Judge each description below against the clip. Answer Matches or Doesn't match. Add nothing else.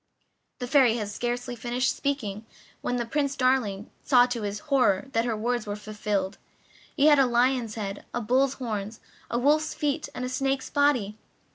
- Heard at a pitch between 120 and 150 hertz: Doesn't match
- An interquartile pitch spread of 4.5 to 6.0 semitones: Doesn't match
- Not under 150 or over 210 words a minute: Matches